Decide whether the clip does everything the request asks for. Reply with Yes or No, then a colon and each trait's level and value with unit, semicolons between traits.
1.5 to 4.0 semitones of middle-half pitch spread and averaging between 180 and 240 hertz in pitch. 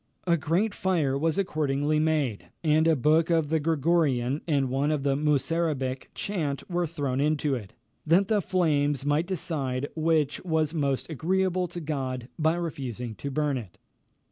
No: average, 3.2 semitones; medium, 150 Hz